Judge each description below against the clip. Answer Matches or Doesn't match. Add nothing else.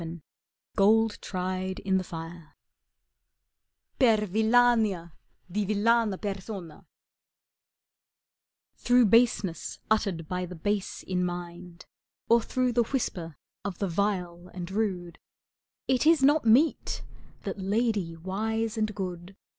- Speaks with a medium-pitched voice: Doesn't match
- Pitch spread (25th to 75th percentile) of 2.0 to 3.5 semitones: Doesn't match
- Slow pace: Matches